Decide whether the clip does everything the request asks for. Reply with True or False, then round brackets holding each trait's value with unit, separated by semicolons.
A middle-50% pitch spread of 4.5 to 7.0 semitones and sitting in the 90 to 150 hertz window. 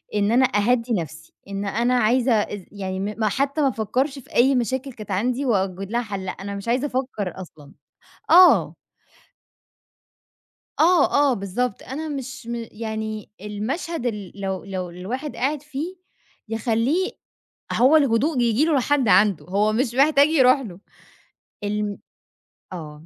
False (4.9 semitones; 230 Hz)